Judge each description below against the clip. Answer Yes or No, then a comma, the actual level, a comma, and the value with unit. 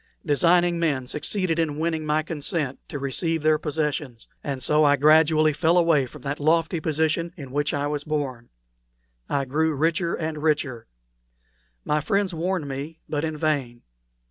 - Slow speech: No, average, 160 wpm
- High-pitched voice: No, medium, 155 Hz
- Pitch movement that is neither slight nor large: No, narrow, 2.3 semitones